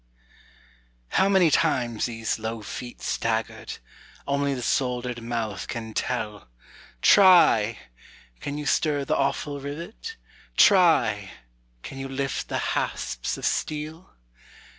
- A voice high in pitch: No, low, 130 Hz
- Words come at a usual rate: No, slow, 115 wpm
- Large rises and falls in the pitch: No, average, 4.7 semitones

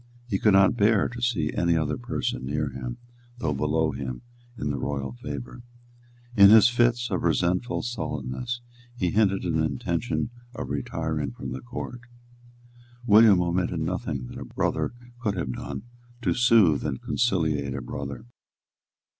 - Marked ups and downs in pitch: Yes, wide, 7.3 semitones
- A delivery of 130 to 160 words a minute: Yes, average, 150 wpm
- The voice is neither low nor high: No, very low, 85 Hz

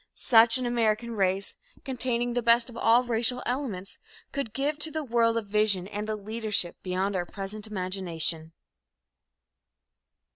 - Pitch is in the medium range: No, high, 225 Hz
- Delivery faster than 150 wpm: No, average, 145 wpm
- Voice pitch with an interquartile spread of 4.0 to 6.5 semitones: No, average, 3.6 semitones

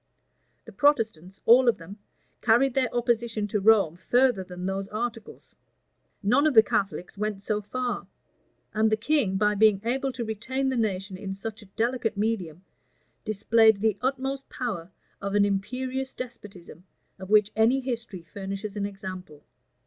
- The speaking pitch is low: No, high, 215 Hz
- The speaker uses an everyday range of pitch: Yes, average, 3.6 semitones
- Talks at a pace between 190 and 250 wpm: No, average, 155 wpm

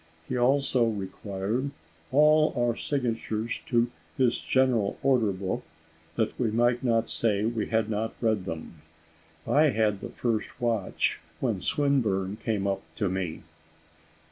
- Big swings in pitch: No, average, 3.6 semitones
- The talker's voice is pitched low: Yes, low, 115 Hz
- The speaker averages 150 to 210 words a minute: No, slow, 135 wpm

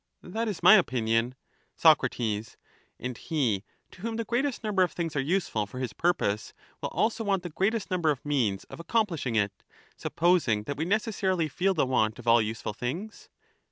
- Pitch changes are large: Yes, wide, 8.7 semitones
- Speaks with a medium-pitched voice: Yes, medium, 160 Hz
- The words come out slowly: No, average, 180 wpm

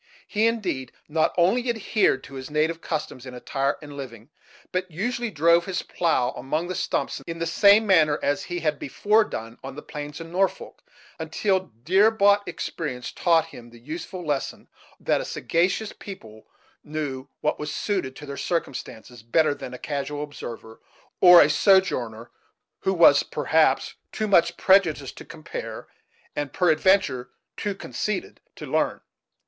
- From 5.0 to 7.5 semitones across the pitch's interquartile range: Yes, wide, 5.4 semitones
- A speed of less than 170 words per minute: Yes, average, 155 wpm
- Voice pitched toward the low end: No, medium, 160 Hz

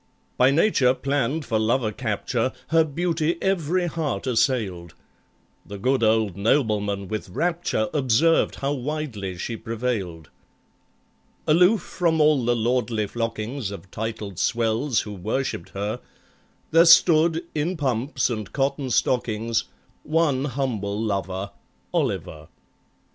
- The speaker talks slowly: Yes, slow, 115 wpm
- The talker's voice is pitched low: Yes, low, 120 Hz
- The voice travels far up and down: Yes, wide, 5.9 semitones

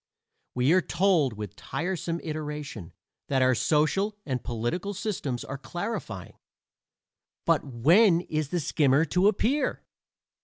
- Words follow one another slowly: Yes, slow, 120 wpm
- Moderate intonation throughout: No, wide, 5.7 semitones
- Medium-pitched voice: Yes, medium, 155 Hz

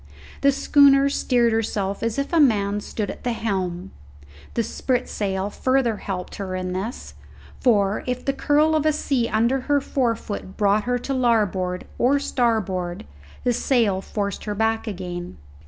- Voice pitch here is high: Yes, high, 225 Hz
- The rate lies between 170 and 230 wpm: No, average, 155 wpm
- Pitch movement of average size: Yes, average, 4.6 semitones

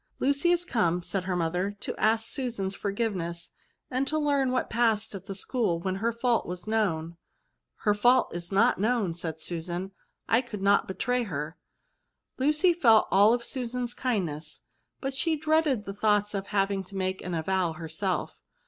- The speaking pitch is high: Yes, high, 205 Hz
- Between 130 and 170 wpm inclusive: No, average, 185 wpm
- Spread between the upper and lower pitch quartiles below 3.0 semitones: No, average, 5.3 semitones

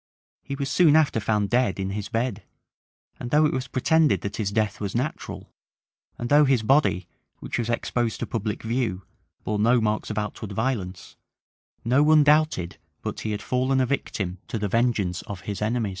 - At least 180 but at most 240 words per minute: Yes, average, 190 wpm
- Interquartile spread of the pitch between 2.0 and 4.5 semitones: Yes, average, 4.2 semitones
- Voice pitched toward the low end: Yes, low, 115 Hz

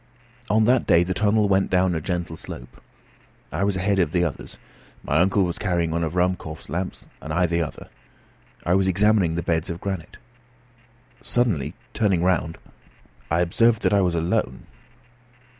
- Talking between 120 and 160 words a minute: No, average, 170 wpm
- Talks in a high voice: No, very low, 90 Hz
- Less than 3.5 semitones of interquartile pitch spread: Yes, average, 2.8 semitones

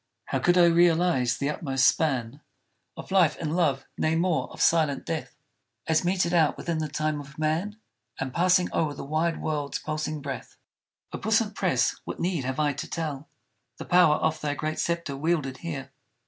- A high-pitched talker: No, medium, 155 Hz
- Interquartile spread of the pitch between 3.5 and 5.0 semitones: No, average, 2.9 semitones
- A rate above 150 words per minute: Yes, average, 180 wpm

